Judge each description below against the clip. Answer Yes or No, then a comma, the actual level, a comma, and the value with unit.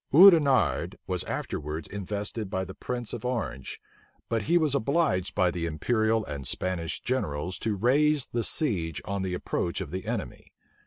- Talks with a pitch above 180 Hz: No, low, 105 Hz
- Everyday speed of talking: Yes, average, 160 wpm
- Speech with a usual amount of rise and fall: No, wide, 6.1 semitones